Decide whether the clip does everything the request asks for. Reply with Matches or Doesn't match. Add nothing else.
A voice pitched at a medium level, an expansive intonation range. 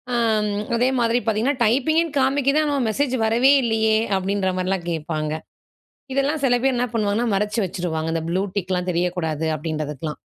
Doesn't match